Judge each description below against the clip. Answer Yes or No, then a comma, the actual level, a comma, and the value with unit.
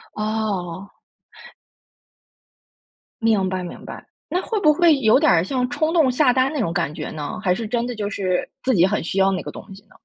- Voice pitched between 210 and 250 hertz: Yes, high, 215 Hz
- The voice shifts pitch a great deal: Yes, wide, 5.7 semitones